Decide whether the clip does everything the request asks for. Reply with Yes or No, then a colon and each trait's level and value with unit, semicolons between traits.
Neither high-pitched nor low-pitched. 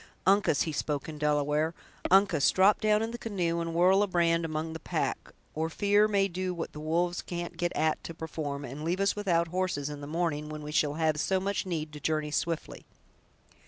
Yes: medium, 165 Hz